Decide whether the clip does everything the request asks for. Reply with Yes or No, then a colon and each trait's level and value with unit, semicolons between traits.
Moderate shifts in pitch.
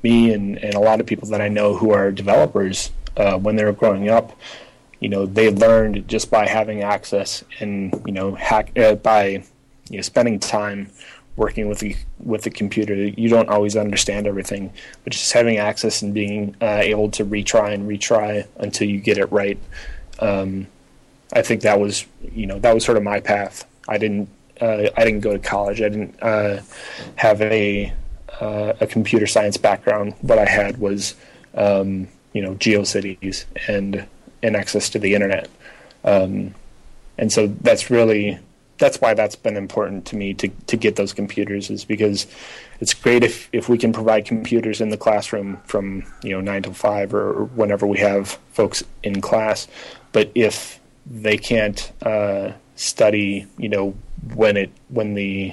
No: narrow, 1.4 semitones